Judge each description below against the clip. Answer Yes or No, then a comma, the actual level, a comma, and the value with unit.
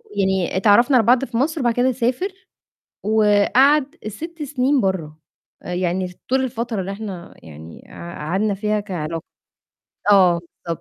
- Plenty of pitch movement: Yes, wide, 5.7 semitones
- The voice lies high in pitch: Yes, high, 210 Hz